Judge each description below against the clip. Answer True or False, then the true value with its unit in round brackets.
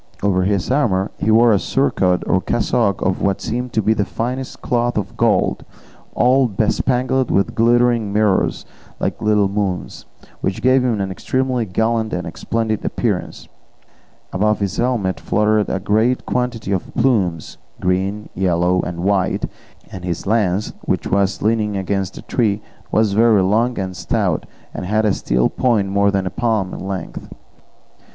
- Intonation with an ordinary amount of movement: True (3.5 semitones)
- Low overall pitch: True (105 Hz)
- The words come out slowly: False (160 wpm)